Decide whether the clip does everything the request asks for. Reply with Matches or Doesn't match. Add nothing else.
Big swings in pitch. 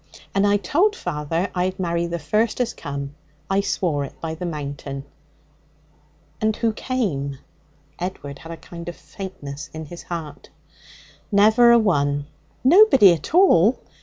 Matches